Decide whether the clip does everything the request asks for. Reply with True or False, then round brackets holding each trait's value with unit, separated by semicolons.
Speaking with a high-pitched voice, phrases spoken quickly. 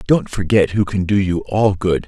False (95 Hz; 230 wpm)